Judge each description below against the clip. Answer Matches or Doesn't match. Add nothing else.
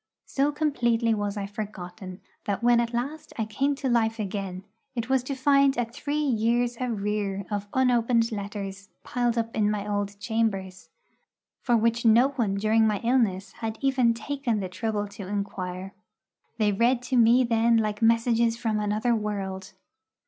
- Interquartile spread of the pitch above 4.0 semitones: Doesn't match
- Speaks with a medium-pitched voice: Doesn't match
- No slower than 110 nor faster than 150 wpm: Doesn't match